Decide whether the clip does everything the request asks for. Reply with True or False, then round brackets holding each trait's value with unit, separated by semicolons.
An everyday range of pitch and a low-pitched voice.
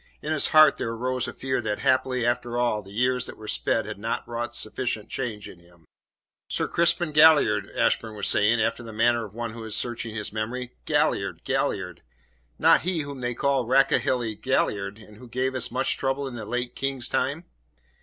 True (3.2 semitones; 120 Hz)